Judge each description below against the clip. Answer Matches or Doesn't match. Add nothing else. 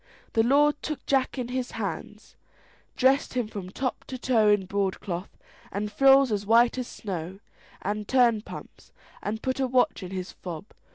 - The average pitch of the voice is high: Matches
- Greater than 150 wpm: Matches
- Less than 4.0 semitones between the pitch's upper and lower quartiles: Doesn't match